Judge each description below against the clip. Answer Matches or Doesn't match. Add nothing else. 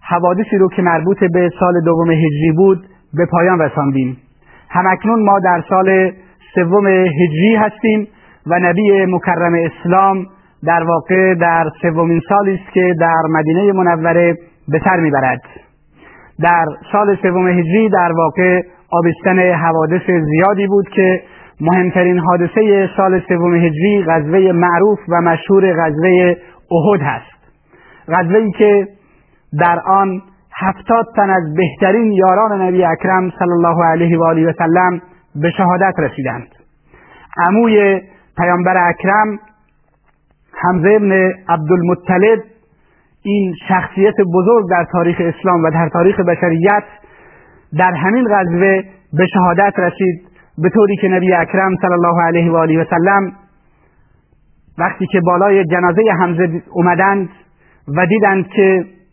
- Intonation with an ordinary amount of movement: Doesn't match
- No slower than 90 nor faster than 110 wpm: Doesn't match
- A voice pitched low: Doesn't match